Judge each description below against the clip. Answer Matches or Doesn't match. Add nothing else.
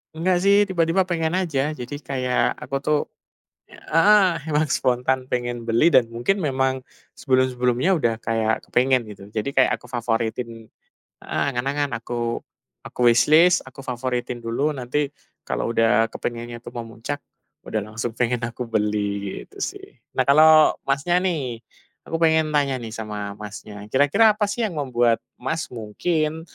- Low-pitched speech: Matches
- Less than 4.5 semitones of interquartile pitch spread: Doesn't match